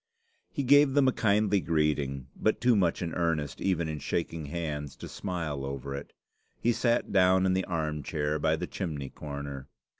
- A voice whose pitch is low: Yes, very low, 80 Hz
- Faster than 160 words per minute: Yes, average, 180 wpm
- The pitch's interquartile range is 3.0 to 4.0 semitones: No, average, 4.9 semitones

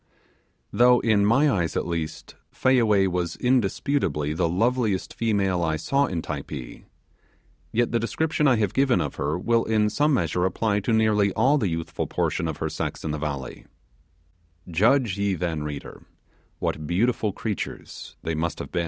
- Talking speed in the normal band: Yes, average, 165 wpm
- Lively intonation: Yes, wide, 6.1 semitones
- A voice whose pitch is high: No, low, 100 Hz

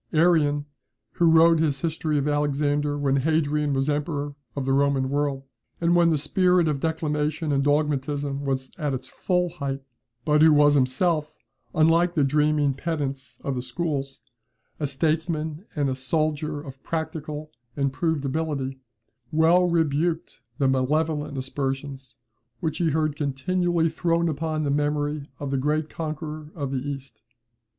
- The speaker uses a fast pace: No, average, 150 wpm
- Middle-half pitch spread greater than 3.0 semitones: No, narrow, 2.5 semitones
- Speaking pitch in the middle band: Yes, medium, 150 Hz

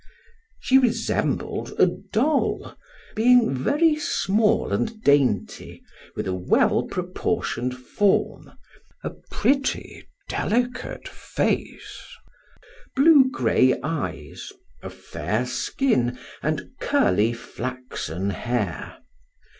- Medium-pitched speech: Yes, medium, 180 Hz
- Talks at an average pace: No, slow, 85 wpm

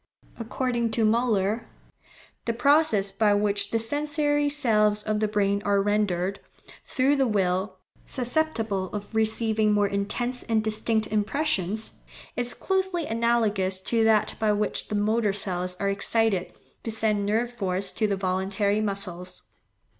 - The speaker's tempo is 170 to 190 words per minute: No, average, 140 wpm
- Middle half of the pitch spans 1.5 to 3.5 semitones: Yes, average, 2.7 semitones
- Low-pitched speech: No, high, 215 Hz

